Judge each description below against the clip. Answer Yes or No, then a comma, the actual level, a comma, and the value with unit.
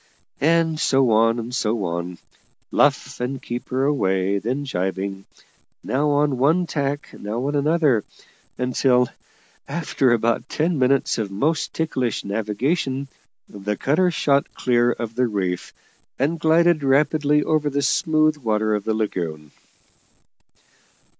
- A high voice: No, low, 130 Hz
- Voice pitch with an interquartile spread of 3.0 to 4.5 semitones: No, wide, 5.4 semitones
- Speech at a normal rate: No, slow, 130 wpm